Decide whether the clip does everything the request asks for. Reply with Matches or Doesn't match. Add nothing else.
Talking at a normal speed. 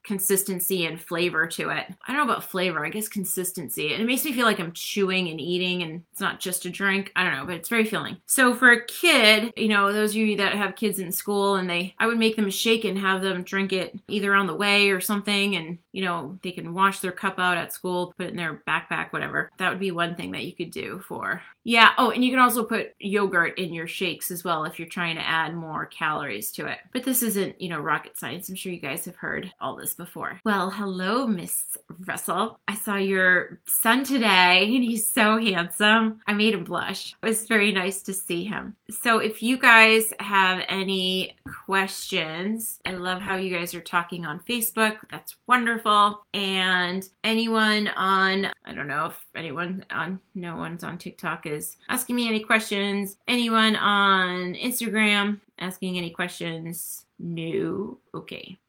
Doesn't match